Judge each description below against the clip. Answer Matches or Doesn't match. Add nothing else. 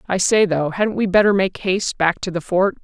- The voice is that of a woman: Matches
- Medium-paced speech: Doesn't match